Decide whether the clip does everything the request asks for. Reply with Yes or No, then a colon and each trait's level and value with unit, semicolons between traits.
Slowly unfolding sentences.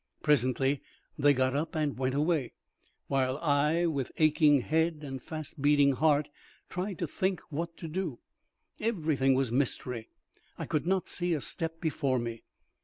No: average, 155 wpm